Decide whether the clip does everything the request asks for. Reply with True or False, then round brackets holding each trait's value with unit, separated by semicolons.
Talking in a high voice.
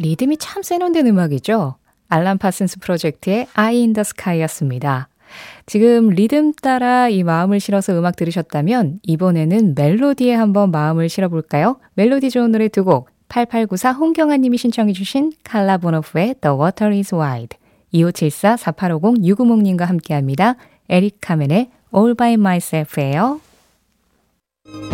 True (195 Hz)